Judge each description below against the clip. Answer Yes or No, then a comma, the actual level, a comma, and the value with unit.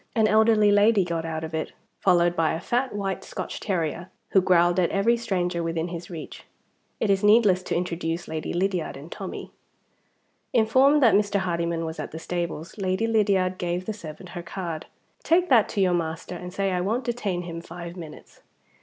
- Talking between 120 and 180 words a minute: No, average, 190 wpm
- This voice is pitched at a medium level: Yes, medium, 180 Hz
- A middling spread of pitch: Yes, average, 3.5 semitones